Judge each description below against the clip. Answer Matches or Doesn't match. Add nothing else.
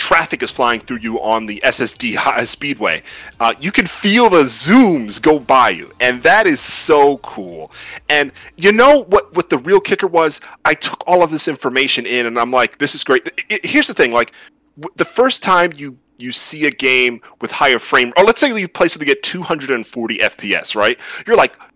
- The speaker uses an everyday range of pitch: Doesn't match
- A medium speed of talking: Doesn't match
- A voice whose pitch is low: Doesn't match